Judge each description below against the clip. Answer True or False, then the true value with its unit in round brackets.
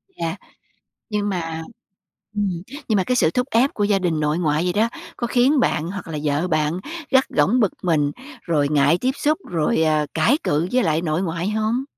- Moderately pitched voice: True (175 Hz)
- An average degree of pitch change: False (5.8 semitones)